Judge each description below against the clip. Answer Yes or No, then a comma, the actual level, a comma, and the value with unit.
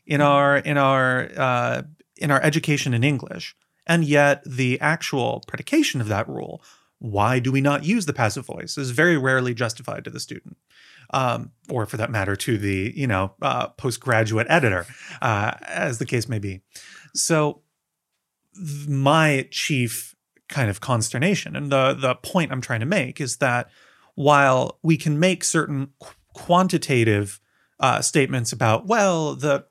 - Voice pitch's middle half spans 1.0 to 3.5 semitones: No, average, 4.1 semitones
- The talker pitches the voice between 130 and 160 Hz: Yes, low, 135 Hz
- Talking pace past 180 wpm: No, average, 160 wpm